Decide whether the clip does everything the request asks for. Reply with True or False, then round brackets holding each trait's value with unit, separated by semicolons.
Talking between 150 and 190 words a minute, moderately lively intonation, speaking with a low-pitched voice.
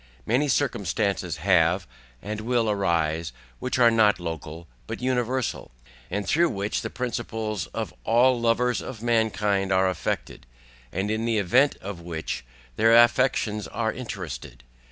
False (135 wpm; 4.0 semitones; 110 Hz)